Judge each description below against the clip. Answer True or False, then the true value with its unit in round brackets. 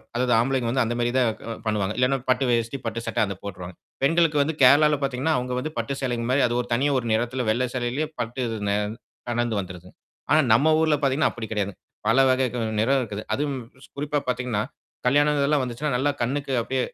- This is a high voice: False (125 Hz)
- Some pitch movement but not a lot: True (3.2 semitones)